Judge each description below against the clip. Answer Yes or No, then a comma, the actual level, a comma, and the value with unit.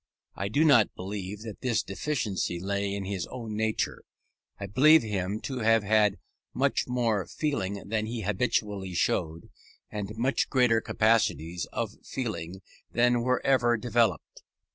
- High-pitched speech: No, low, 110 Hz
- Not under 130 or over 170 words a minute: Yes, average, 140 wpm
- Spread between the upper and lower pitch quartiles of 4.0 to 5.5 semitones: No, average, 3.5 semitones